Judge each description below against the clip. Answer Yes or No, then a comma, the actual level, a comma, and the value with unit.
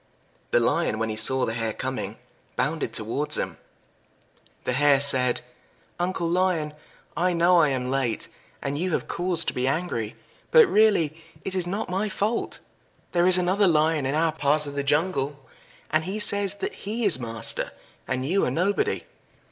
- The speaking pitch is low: No, medium, 160 Hz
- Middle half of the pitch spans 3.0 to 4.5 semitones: No, wide, 5.5 semitones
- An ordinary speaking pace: Yes, average, 170 wpm